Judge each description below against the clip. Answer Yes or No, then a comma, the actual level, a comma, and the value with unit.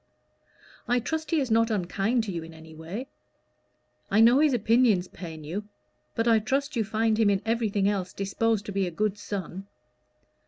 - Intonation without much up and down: No, average, 3.2 semitones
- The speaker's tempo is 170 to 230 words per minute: Yes, average, 185 wpm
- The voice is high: Yes, high, 215 Hz